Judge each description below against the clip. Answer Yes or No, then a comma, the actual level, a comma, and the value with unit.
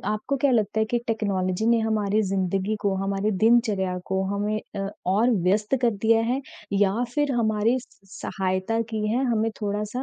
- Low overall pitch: No, high, 215 Hz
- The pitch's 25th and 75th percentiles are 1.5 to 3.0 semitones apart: Yes, narrow, 2.6 semitones